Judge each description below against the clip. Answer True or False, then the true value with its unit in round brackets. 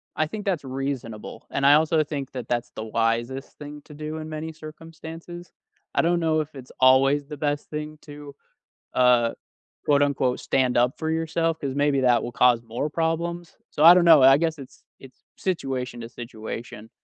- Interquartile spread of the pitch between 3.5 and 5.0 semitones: True (3.9 semitones)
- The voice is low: False (145 Hz)